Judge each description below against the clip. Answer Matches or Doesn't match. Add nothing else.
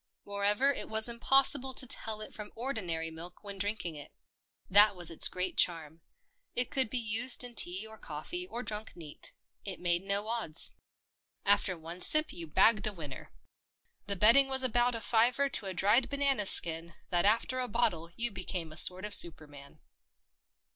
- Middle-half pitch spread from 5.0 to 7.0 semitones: Matches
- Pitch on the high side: Matches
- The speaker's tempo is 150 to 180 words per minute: Matches